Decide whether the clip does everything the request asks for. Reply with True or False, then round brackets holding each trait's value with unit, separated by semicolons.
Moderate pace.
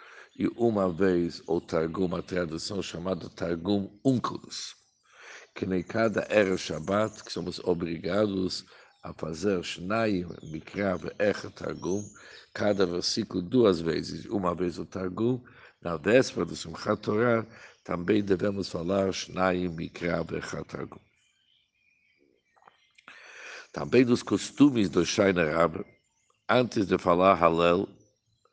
False (90 wpm)